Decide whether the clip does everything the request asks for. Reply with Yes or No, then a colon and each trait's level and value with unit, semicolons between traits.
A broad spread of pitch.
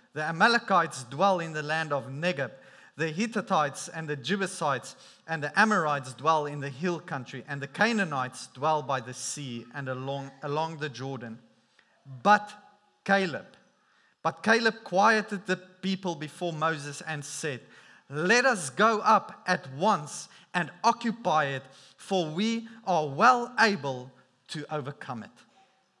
Yes: wide, 5.8 semitones